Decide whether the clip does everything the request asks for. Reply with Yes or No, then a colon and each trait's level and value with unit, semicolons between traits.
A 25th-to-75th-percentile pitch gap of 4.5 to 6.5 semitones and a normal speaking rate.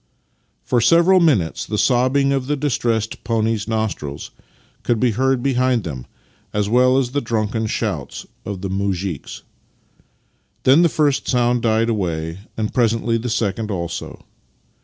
No: average, 3.7 semitones; average, 145 wpm